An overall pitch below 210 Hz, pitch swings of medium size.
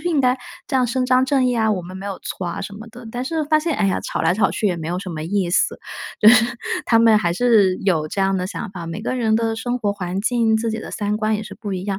No: high, 215 Hz; average, 4.2 semitones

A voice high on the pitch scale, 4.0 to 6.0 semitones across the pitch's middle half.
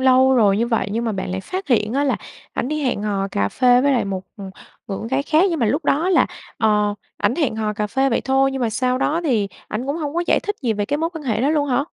Yes: very high, 250 Hz; average, 5.1 semitones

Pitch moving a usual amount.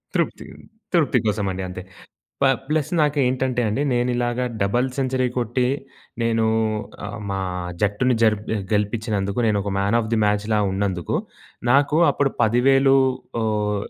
Yes: average, 3.9 semitones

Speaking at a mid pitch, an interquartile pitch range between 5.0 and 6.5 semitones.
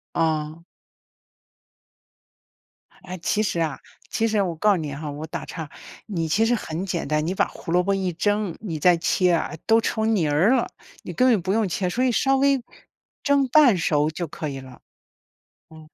Yes: medium, 180 Hz; wide, 5.5 semitones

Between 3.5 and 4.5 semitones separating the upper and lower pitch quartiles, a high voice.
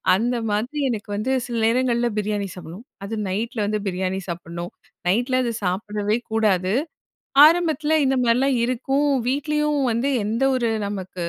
Yes: average, 4.2 semitones; high, 230 Hz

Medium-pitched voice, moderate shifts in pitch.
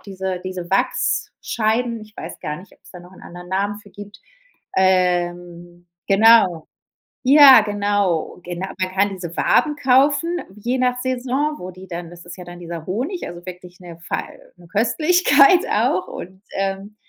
No: high, 195 Hz; average, 5.0 semitones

